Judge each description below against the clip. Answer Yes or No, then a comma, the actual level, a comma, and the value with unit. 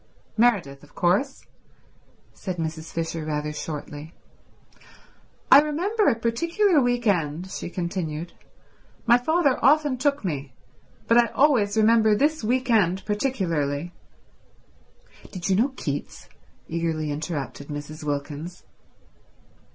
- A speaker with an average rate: No, slow, 110 wpm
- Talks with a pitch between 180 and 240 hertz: Yes, medium, 185 Hz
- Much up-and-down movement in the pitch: Yes, wide, 7.9 semitones